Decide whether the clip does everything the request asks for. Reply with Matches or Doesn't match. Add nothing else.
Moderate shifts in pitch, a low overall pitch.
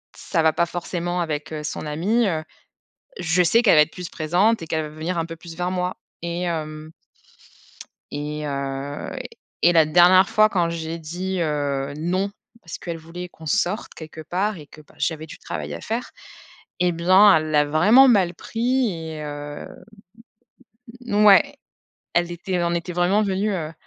Doesn't match